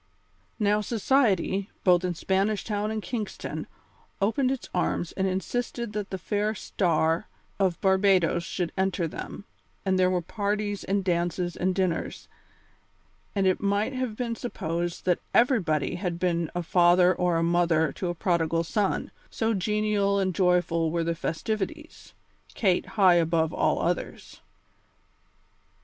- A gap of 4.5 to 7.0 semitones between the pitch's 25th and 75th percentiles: No, average, 3.3 semitones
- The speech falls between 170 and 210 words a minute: No, average, 140 wpm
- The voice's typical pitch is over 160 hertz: Yes, high, 190 Hz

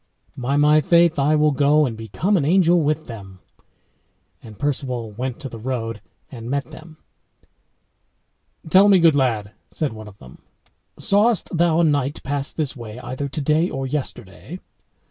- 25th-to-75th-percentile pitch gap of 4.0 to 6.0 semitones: Yes, average, 4.8 semitones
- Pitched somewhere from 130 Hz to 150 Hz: Yes, medium, 140 Hz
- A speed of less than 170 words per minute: Yes, average, 160 wpm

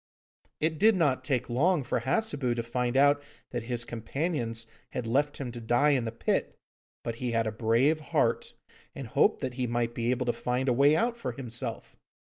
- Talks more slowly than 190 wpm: No, average, 200 wpm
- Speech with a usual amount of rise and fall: Yes, average, 3.5 semitones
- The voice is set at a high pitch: No, low, 125 Hz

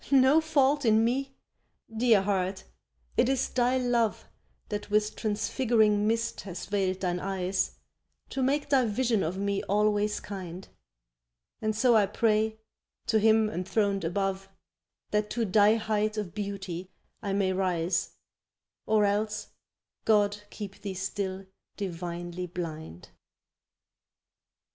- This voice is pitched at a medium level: No, high, 205 Hz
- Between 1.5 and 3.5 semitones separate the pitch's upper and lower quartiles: Yes, average, 2.8 semitones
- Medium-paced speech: No, slow, 125 wpm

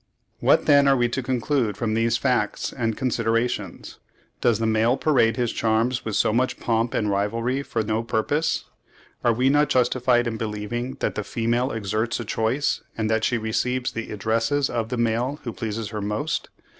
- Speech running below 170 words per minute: No, average, 180 wpm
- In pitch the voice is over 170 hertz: No, low, 115 Hz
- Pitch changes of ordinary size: No, narrow, 2.3 semitones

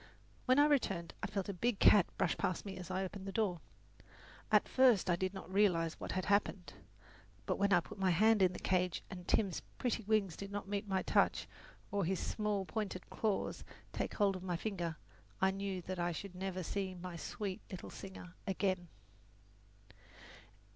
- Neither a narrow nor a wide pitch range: No, narrow, 2.0 semitones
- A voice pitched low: No, high, 190 Hz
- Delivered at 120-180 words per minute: No, average, 190 wpm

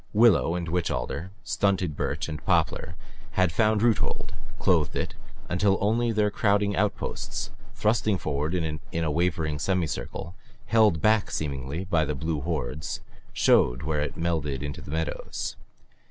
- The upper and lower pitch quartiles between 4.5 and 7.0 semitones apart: Yes, average, 5.0 semitones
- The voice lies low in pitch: Yes, very low, 85 Hz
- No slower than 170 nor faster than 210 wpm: No, average, 140 wpm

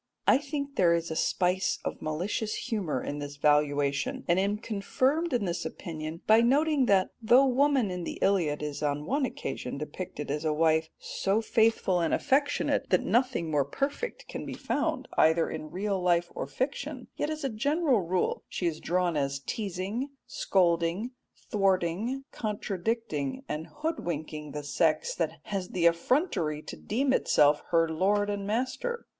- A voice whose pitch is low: No, high, 190 Hz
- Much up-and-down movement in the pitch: Yes, wide, 7.6 semitones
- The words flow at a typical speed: Yes, average, 160 wpm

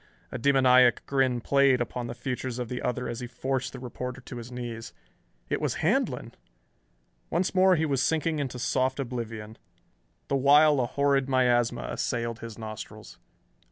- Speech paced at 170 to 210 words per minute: No, average, 160 wpm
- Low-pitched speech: Yes, low, 125 Hz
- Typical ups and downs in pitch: No, narrow, 2.3 semitones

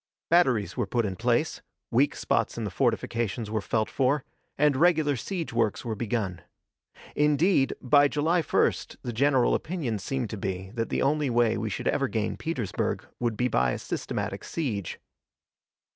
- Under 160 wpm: No, average, 165 wpm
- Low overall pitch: Yes, low, 120 Hz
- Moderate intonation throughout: Yes, average, 5.0 semitones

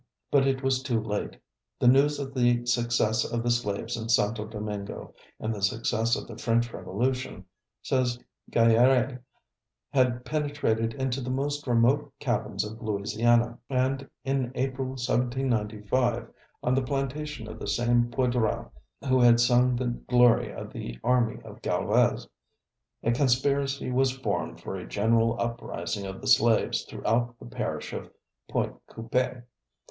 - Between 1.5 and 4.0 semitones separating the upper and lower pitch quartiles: Yes, narrow, 2.4 semitones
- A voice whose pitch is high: No, low, 120 Hz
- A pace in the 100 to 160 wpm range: Yes, average, 145 wpm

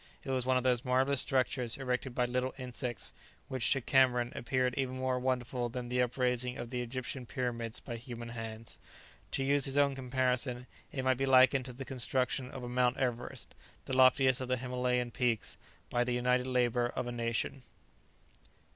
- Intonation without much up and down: Yes, narrow, 1.1 semitones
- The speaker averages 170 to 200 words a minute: Yes, average, 180 wpm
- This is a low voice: Yes, low, 125 Hz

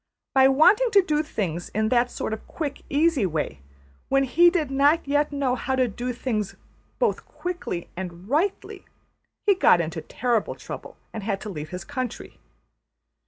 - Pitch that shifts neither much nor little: No, wide, 6.7 semitones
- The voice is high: Yes, very high, 255 Hz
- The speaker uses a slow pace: No, average, 165 wpm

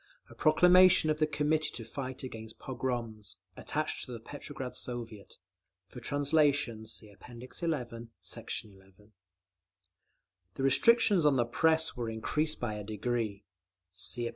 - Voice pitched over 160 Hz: No, low, 125 Hz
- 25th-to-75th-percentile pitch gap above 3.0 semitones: Yes, average, 5.3 semitones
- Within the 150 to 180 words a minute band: No, average, 140 wpm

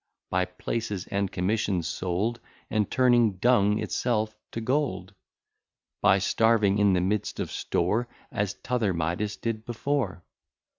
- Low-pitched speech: Yes, low, 105 Hz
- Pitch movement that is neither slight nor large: Yes, average, 3.6 semitones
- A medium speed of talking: No, slow, 130 wpm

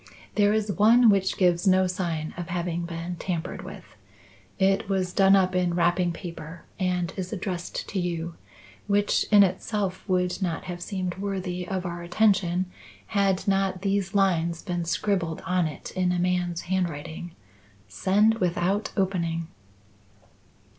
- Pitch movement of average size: No, narrow, 2.1 semitones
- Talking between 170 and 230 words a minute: No, average, 145 wpm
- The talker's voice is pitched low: No, medium, 180 Hz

